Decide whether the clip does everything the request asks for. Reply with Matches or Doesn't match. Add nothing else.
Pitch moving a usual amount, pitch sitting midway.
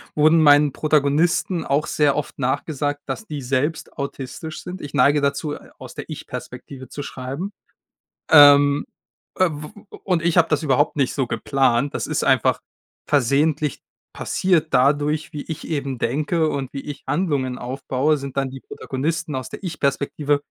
Doesn't match